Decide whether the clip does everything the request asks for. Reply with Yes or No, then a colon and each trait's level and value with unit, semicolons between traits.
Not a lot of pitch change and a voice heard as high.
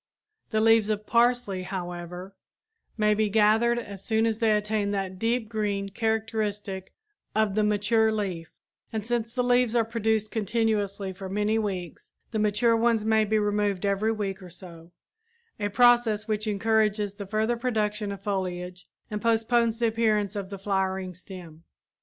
Yes: narrow, 2.2 semitones; high, 210 Hz